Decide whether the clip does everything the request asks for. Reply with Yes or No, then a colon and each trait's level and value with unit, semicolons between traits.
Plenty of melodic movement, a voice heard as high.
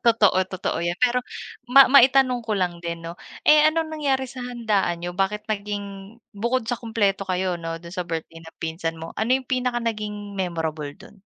Yes: wide, 5.8 semitones; high, 205 Hz